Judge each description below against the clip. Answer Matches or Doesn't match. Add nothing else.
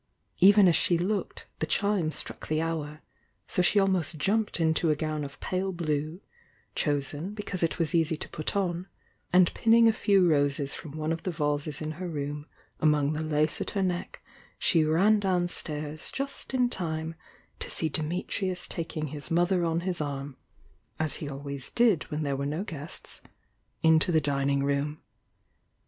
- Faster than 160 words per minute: Matches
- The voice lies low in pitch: Doesn't match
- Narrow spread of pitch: Doesn't match